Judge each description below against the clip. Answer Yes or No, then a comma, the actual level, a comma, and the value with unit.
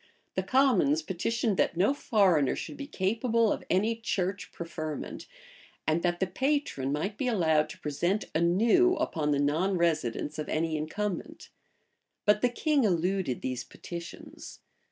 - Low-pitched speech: No, medium, 185 Hz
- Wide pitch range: Yes, wide, 6.1 semitones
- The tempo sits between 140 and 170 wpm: Yes, average, 145 wpm